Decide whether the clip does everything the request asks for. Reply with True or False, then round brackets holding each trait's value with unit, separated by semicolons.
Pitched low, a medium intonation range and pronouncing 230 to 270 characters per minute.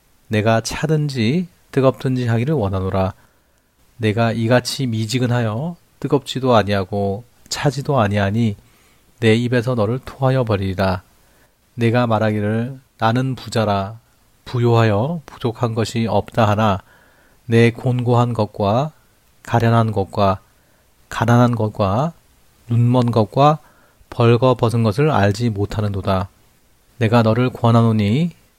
True (115 Hz; 3.0 semitones; 250 characters per minute)